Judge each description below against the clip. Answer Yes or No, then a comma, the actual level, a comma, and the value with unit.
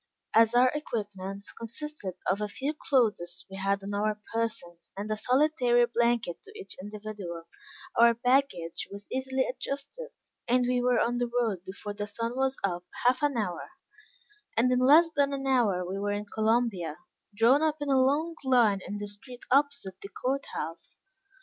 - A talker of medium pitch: No, high, 235 Hz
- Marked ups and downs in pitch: No, average, 4.5 semitones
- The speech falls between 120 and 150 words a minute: No, average, 175 wpm